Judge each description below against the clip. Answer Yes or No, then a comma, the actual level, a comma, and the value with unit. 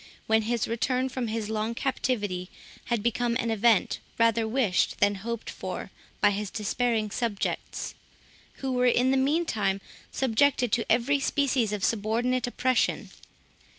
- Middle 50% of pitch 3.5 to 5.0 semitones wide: No, average, 2.9 semitones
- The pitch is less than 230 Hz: No, high, 235 Hz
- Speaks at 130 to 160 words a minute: Yes, average, 140 wpm